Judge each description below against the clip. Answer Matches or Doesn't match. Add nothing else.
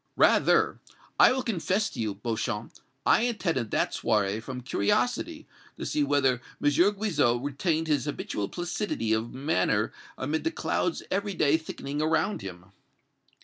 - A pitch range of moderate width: Doesn't match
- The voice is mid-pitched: Matches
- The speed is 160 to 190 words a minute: Doesn't match